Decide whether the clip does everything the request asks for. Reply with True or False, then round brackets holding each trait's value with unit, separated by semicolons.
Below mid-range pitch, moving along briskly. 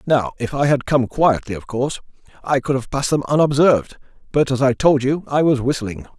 True (130 Hz; 215 wpm)